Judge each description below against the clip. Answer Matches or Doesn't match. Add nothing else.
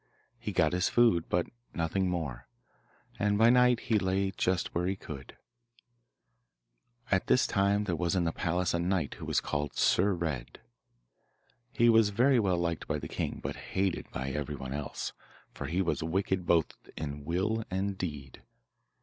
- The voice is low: Matches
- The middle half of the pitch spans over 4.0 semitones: Doesn't match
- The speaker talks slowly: Doesn't match